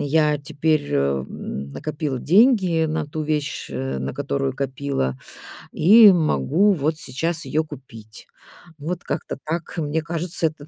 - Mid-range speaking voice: Yes, medium, 150 Hz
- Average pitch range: Yes, average, 3.0 semitones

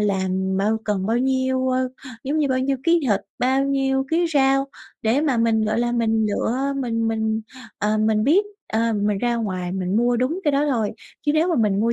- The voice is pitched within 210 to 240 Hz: Yes, high, 235 Hz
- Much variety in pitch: No, average, 3.9 semitones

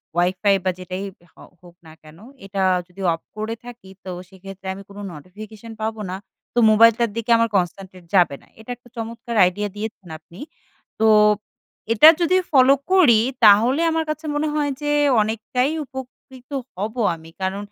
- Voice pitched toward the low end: No, high, 215 Hz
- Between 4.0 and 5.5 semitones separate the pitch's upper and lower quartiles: Yes, average, 4.3 semitones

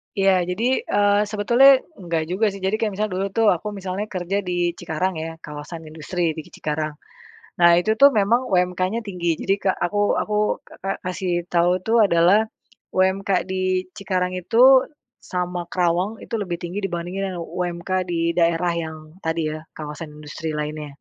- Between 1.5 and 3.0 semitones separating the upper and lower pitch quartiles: Yes, average, 2.7 semitones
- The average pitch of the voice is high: No, medium, 180 Hz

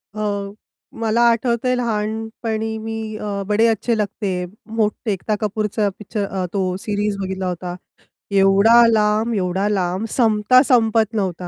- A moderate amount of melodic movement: No, narrow, 2.0 semitones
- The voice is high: Yes, high, 210 Hz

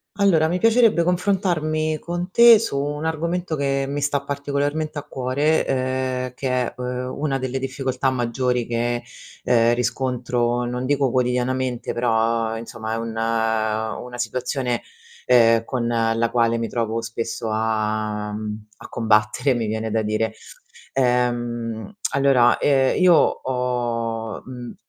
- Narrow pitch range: No, average, 3.3 semitones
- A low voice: Yes, low, 125 Hz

